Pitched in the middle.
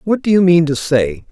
Yes: medium, 160 Hz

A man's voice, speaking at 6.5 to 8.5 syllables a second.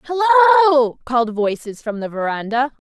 No: female; 8.2 syllables/s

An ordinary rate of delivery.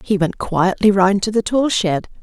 No: fast, 215 wpm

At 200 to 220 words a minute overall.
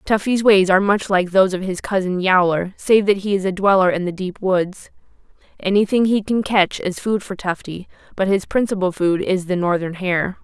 Yes: fast, 205 wpm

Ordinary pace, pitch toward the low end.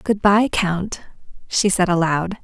No: average, 150 wpm; high, 190 Hz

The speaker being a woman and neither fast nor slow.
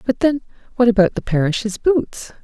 Yes: female; average, 175 wpm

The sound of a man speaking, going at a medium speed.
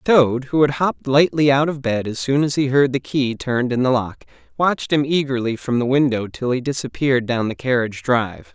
No: male; fast, 230 wpm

